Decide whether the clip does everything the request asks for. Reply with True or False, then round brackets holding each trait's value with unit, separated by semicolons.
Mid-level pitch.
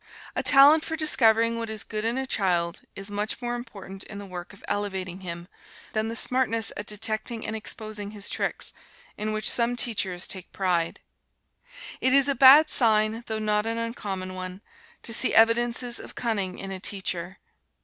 False (215 Hz)